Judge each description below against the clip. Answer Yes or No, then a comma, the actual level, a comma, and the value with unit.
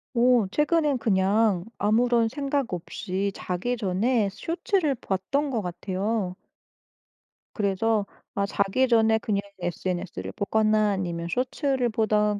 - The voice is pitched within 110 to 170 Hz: No, high, 215 Hz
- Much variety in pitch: No, average, 4.2 semitones